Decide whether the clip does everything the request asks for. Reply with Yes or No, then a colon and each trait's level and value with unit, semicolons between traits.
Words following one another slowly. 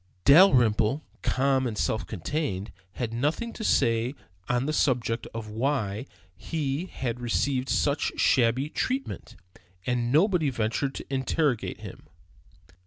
Yes: slow, 120 wpm